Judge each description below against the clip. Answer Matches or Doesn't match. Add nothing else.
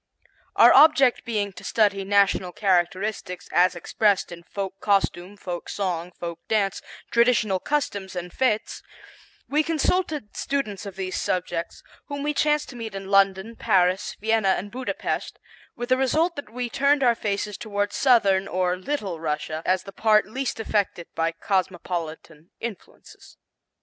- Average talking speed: Matches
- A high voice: Matches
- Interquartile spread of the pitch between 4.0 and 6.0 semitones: Matches